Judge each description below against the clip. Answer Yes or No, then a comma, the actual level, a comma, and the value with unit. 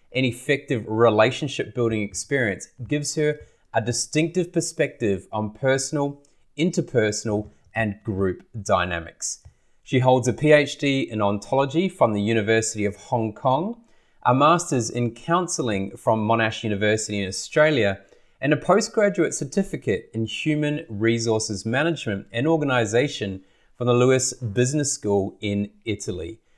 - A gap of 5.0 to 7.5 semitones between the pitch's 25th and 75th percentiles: Yes, wide, 5.6 semitones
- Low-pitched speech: Yes, low, 120 Hz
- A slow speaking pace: Yes, slow, 120 wpm